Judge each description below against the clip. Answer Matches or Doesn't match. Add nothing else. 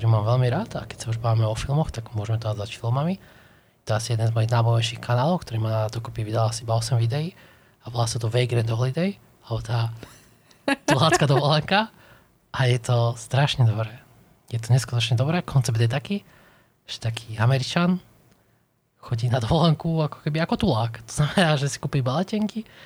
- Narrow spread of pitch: Doesn't match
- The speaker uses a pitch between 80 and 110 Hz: Doesn't match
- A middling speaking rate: Doesn't match